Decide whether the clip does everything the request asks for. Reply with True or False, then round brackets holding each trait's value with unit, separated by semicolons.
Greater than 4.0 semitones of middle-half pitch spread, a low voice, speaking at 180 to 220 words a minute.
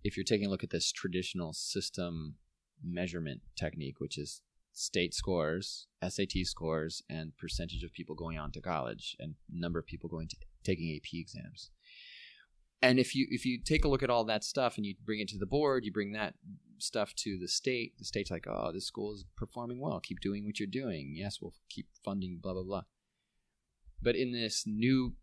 True (4.4 semitones; 95 Hz; 200 wpm)